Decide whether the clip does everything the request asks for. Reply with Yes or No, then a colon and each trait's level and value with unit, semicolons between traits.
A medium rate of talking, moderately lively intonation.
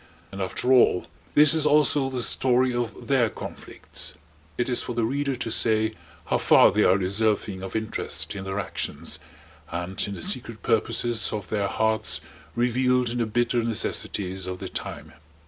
Yes: average, 170 wpm; average, 3.8 semitones